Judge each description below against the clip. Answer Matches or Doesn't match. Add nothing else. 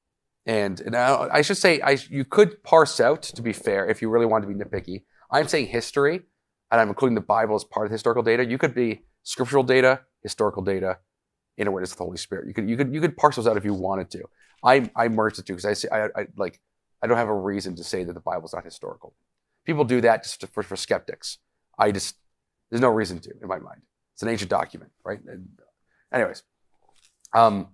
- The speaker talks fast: Matches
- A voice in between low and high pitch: Doesn't match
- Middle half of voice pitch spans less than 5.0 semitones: Doesn't match